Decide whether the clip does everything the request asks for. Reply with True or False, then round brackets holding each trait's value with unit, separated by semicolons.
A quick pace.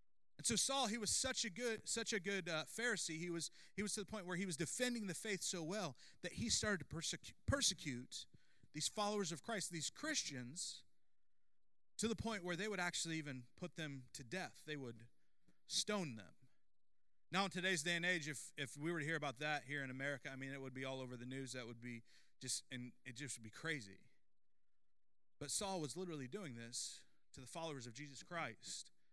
True (215 wpm)